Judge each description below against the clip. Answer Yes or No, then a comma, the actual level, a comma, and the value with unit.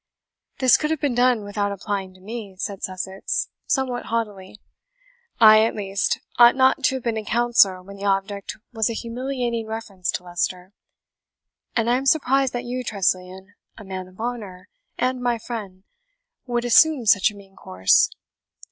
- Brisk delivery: No, average, 165 wpm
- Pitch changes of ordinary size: Yes, average, 4.0 semitones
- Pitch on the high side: Yes, high, 220 Hz